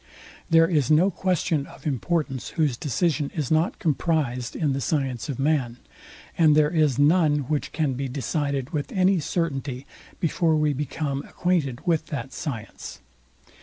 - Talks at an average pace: Yes, average, 150 wpm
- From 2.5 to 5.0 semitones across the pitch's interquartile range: Yes, average, 3.1 semitones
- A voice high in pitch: No, medium, 150 Hz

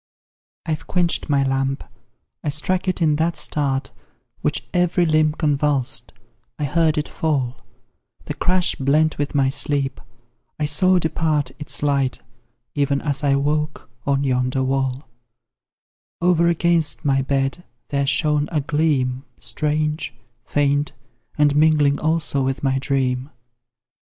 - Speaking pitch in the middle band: Yes, medium, 145 Hz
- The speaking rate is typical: No, slow, 130 wpm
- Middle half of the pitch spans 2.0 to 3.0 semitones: Yes, narrow, 2.4 semitones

